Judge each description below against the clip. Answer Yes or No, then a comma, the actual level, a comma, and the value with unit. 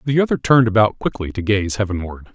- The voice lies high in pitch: No, low, 105 Hz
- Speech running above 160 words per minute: Yes, fast, 205 wpm